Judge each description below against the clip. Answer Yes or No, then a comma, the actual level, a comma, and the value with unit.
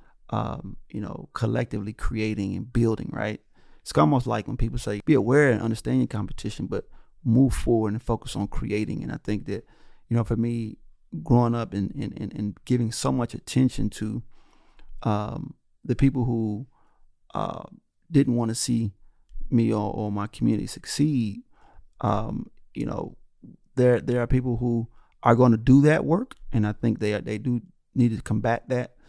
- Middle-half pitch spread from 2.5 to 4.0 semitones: Yes, average, 2.9 semitones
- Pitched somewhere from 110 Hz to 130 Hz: Yes, low, 115 Hz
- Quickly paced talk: No, average, 170 wpm